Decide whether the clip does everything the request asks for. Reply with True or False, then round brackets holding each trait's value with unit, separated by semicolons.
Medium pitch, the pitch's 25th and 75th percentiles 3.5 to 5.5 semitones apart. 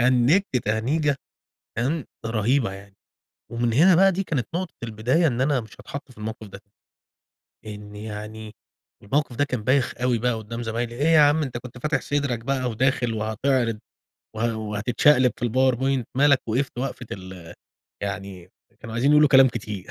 False (120 Hz; 4.0 semitones)